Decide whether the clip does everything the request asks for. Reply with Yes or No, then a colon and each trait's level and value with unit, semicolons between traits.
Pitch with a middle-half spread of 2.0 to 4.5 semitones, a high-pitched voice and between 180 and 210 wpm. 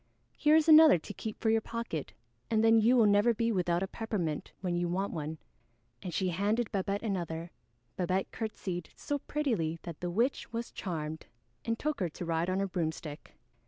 No: average, 4.9 semitones; high, 195 Hz; average, 190 wpm